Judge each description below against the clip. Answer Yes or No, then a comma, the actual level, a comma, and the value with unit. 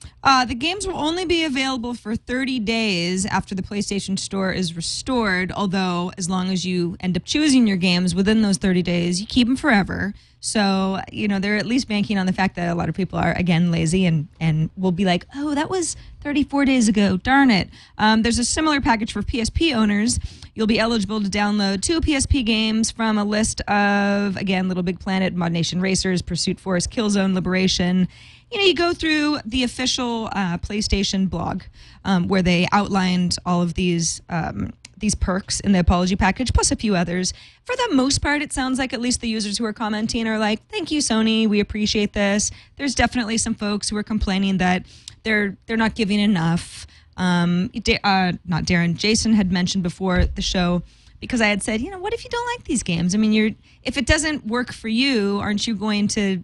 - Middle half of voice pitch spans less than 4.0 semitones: No, average, 4.3 semitones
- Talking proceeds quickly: Yes, fast, 210 wpm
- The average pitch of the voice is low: No, high, 205 Hz